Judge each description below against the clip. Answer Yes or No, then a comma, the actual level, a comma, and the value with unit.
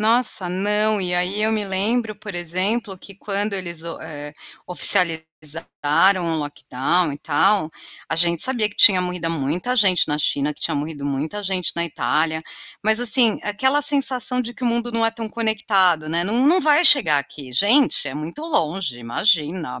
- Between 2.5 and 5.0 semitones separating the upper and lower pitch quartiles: No, wide, 5.4 semitones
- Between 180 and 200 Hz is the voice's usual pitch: Yes, medium, 185 Hz